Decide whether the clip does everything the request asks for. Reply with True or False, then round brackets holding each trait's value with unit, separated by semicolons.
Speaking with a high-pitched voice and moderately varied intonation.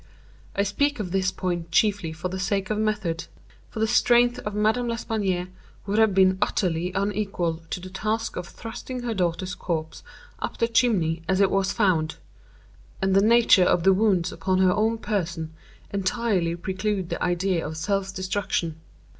True (195 Hz; 3.2 semitones)